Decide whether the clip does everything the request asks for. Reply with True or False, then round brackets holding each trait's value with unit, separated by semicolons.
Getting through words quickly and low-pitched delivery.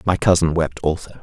False (195 wpm; 85 Hz)